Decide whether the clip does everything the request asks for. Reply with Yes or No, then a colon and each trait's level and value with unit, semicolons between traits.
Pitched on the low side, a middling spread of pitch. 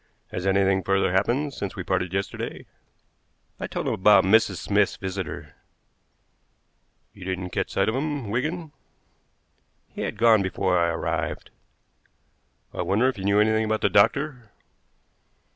Yes: low, 100 Hz; average, 3.3 semitones